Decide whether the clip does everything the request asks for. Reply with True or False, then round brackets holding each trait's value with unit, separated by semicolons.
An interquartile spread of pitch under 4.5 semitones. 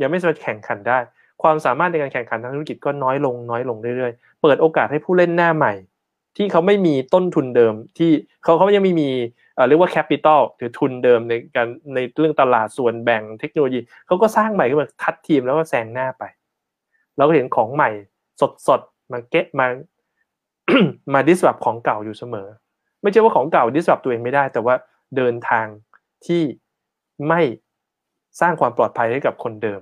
False (5.4 semitones)